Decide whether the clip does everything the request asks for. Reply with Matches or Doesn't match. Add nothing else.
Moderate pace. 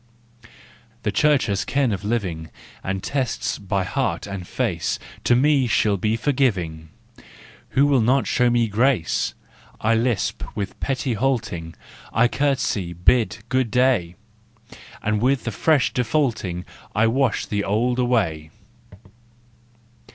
Doesn't match